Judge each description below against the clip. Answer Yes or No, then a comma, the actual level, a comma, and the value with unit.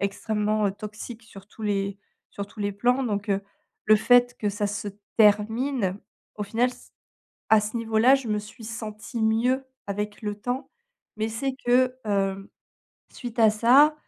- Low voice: No, high, 215 Hz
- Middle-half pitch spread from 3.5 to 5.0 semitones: No, average, 2.8 semitones